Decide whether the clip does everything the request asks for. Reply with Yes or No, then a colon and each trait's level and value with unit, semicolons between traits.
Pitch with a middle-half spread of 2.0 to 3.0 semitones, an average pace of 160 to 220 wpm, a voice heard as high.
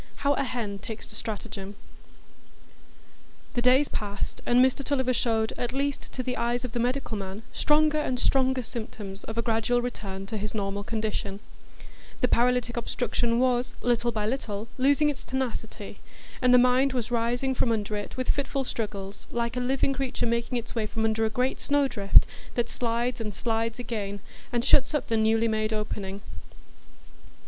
Yes: average, 2.7 semitones; average, 175 wpm; high, 235 Hz